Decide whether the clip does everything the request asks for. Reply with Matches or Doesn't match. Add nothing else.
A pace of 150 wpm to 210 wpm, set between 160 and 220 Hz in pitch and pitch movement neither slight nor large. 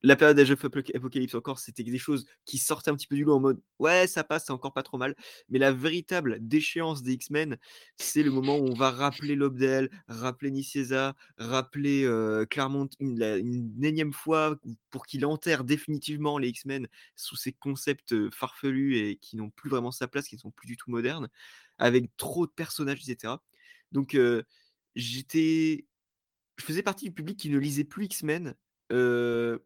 Doesn't match